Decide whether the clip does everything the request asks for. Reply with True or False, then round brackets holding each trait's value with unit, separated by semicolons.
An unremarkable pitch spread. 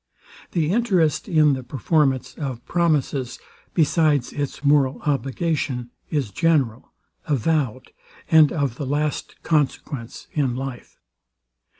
True (3.2 semitones)